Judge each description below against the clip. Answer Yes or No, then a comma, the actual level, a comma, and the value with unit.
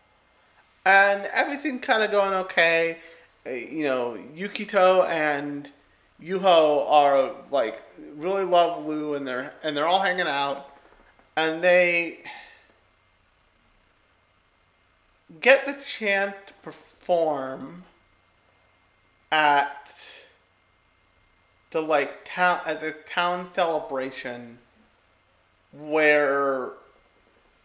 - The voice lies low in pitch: No, medium, 150 Hz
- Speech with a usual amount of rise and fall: No, wide, 8.4 semitones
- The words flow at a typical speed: No, slow, 85 wpm